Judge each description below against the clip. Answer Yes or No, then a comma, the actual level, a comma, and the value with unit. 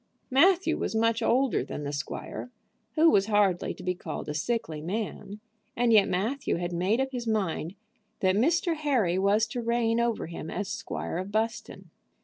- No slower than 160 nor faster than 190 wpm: Yes, average, 175 wpm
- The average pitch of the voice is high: Yes, high, 220 Hz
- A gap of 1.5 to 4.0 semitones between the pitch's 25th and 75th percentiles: No, average, 4.6 semitones